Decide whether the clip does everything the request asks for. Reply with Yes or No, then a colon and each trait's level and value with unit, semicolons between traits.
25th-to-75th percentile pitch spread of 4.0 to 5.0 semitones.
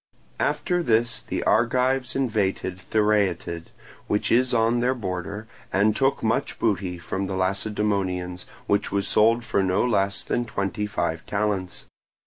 No: average, 3.4 semitones